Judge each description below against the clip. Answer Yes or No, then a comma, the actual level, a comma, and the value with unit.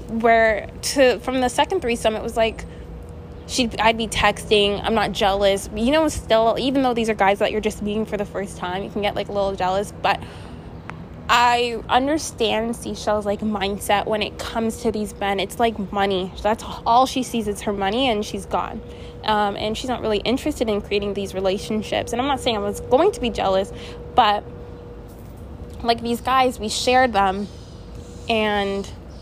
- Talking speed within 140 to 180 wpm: No, average, 190 wpm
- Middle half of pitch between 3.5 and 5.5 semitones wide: No, average, 2.9 semitones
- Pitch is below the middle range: No, high, 215 Hz